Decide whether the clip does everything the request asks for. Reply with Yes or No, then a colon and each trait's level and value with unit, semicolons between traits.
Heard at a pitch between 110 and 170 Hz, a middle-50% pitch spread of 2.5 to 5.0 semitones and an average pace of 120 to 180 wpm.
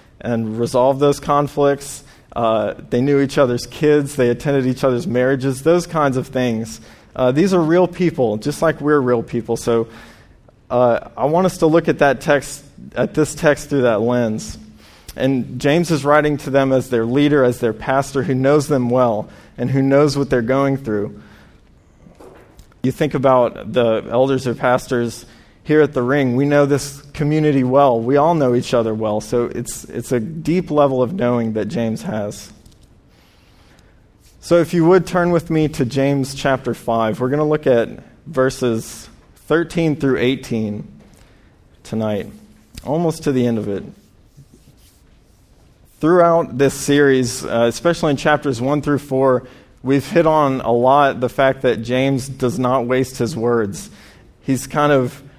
Yes: low, 130 Hz; average, 3.6 semitones; average, 170 wpm